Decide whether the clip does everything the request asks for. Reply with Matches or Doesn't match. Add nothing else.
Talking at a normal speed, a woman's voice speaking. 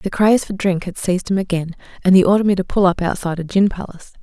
Doesn't match